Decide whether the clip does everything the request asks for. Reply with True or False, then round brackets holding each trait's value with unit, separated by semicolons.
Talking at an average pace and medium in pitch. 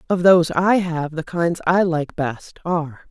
True (195 wpm; 170 Hz)